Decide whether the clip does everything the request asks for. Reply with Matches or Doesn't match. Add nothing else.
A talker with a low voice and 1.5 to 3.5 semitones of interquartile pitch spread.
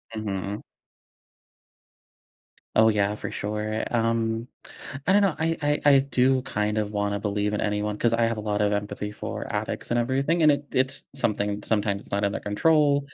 Doesn't match